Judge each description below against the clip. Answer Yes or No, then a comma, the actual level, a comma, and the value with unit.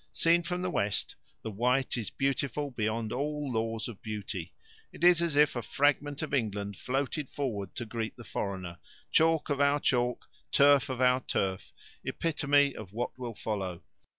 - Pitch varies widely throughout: No, average, 4.9 semitones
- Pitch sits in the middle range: No, low, 125 Hz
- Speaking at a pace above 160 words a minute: Yes, average, 170 wpm